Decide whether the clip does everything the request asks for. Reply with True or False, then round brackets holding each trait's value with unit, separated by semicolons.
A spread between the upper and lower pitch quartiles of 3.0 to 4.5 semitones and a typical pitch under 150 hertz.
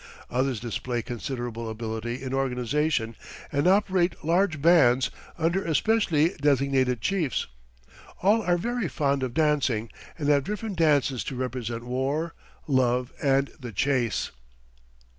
False (4.9 semitones; 135 Hz)